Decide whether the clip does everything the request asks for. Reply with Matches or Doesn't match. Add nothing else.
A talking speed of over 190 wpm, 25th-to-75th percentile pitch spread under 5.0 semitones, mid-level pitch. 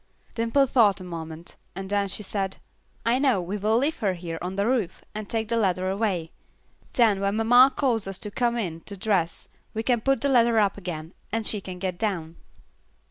Doesn't match